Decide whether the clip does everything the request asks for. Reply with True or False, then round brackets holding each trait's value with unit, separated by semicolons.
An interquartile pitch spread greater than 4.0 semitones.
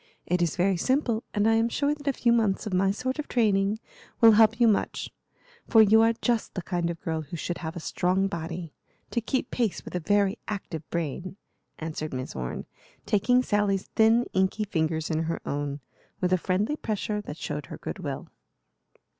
True (4.9 semitones)